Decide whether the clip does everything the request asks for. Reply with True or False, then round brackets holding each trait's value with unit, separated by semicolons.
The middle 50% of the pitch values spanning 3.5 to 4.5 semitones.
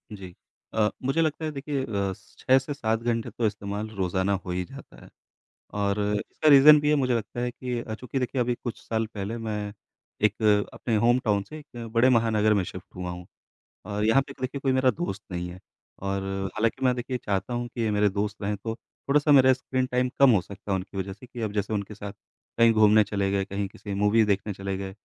True (4.0 semitones)